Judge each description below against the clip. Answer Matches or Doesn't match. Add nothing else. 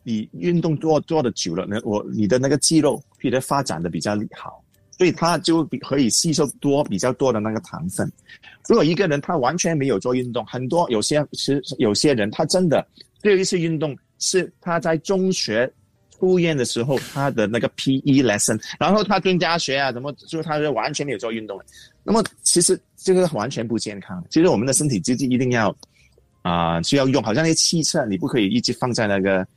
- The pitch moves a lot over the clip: Matches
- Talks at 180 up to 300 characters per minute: Doesn't match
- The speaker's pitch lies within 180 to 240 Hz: Doesn't match